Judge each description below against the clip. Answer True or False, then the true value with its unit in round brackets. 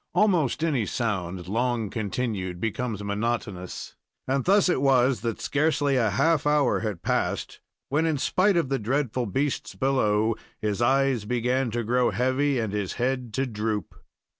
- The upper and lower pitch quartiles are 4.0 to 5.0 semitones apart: True (4.3 semitones)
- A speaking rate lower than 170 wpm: True (155 wpm)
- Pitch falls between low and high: False (125 Hz)